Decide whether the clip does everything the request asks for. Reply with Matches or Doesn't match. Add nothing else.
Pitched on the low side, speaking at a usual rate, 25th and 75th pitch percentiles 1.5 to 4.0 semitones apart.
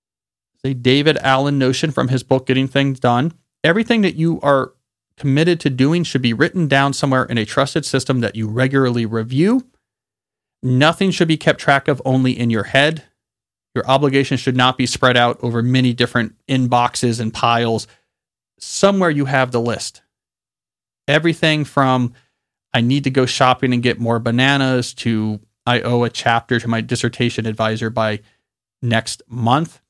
Matches